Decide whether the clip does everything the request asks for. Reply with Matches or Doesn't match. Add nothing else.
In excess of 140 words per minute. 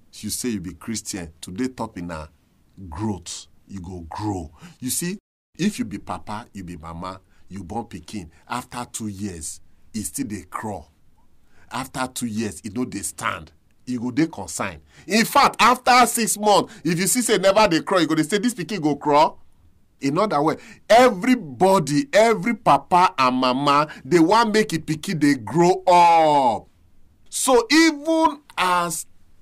Matches